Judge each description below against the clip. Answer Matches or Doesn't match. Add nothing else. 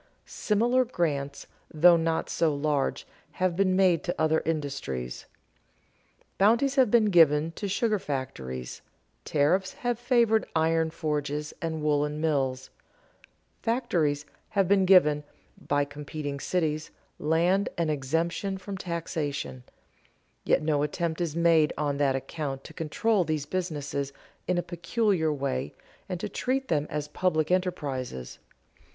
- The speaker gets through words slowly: Matches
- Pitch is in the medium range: Matches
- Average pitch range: Matches